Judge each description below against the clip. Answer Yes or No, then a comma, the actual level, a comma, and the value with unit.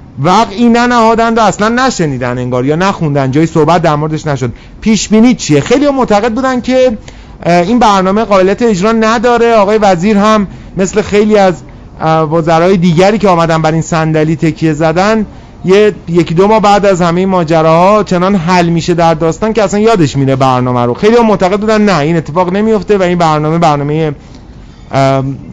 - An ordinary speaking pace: No, fast, 165 wpm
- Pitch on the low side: No, medium, 185 Hz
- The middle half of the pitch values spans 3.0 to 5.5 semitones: Yes, average, 5.2 semitones